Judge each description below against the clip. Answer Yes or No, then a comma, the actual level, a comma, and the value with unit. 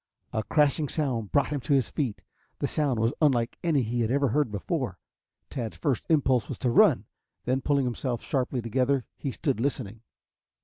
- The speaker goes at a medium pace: Yes, average, 180 wpm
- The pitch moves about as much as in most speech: Yes, average, 3.4 semitones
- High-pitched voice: No, low, 130 Hz